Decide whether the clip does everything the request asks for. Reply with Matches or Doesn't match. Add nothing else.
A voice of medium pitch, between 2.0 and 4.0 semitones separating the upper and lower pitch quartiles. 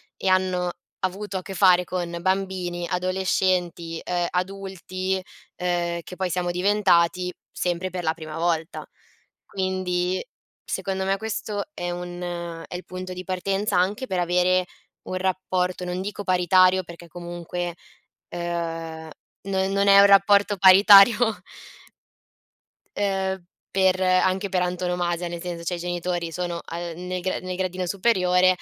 Doesn't match